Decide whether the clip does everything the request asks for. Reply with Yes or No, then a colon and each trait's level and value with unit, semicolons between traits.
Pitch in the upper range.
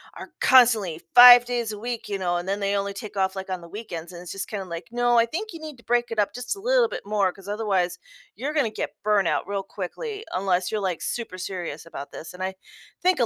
Yes: high, 205 Hz